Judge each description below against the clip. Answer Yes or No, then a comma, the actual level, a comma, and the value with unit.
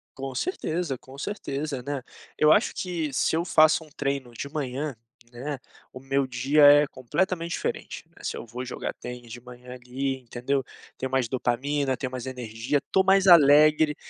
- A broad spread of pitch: No, average, 3.3 semitones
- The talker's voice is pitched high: No, low, 135 Hz